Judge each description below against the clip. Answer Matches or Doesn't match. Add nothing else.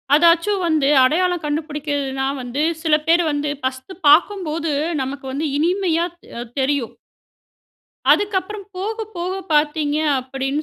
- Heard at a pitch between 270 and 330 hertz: Matches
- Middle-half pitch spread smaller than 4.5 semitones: Matches